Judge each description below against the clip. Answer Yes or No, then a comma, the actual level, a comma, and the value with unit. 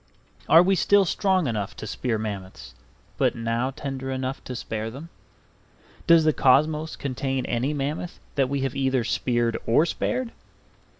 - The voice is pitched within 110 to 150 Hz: Yes, low, 135 Hz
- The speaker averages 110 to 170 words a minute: Yes, average, 155 wpm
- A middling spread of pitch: Yes, average, 4.7 semitones